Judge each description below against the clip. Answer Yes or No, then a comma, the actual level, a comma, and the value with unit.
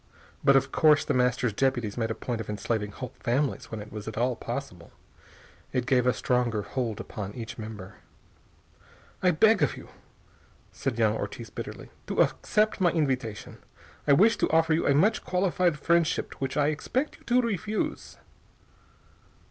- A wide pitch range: Yes, wide, 6.4 semitones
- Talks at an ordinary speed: Yes, average, 165 wpm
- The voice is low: Yes, low, 130 Hz